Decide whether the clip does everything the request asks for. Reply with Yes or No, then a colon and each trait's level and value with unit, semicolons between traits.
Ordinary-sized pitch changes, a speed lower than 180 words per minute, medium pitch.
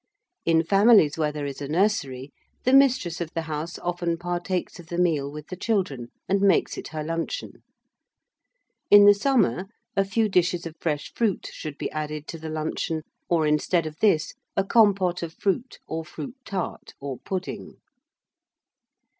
Yes: average, 4.2 semitones; average, 165 wpm; medium, 170 Hz